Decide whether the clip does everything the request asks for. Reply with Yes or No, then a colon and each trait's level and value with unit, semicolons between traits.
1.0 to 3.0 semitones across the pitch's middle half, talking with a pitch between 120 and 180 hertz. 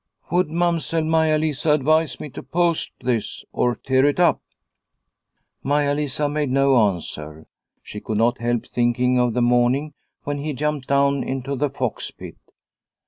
No: average, 3.7 semitones; medium, 140 Hz